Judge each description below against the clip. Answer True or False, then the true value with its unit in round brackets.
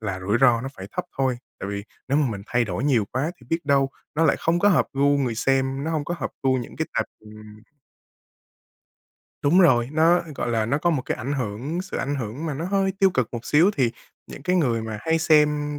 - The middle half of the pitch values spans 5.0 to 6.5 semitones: True (5.4 semitones)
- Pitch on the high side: False (135 Hz)